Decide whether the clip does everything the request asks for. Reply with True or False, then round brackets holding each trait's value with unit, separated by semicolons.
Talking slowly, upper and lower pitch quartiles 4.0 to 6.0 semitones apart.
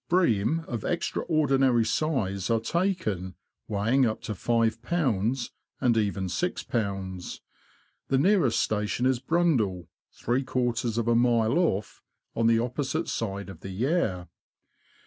True (125 wpm; 4.6 semitones)